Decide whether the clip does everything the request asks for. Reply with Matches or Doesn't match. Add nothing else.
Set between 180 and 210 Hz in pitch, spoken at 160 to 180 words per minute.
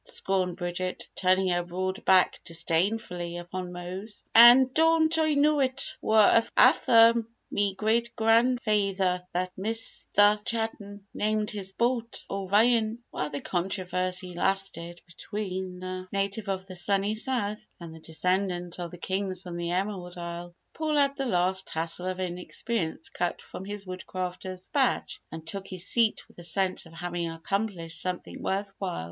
Doesn't match